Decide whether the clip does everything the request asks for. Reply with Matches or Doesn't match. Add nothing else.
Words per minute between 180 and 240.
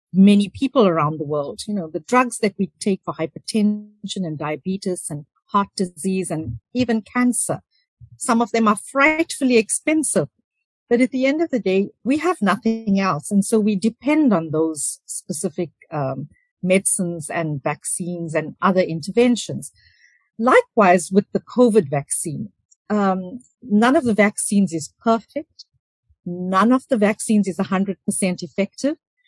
Doesn't match